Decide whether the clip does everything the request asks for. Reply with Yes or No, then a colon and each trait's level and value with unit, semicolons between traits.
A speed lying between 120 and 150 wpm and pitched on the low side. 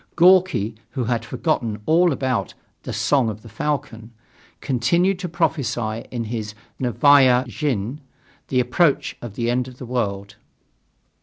Yes: average, 140 wpm; low, 125 Hz